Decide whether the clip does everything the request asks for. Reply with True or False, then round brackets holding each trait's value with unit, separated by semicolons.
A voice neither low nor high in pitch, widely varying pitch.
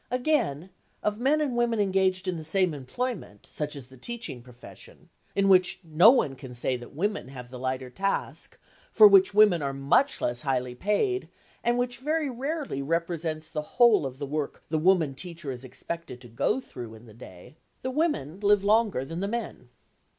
True (170 Hz; 8.4 semitones)